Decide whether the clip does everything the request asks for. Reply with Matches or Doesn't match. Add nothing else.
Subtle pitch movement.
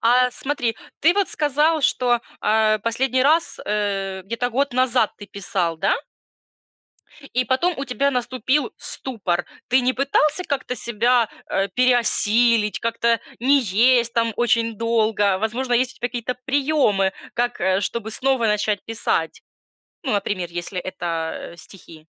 Doesn't match